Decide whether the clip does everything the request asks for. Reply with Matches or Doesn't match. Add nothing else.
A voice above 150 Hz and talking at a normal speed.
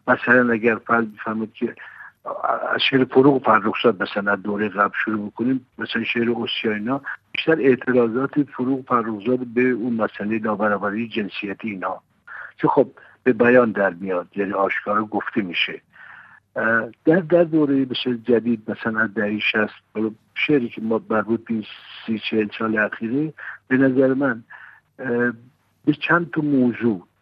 Doesn't match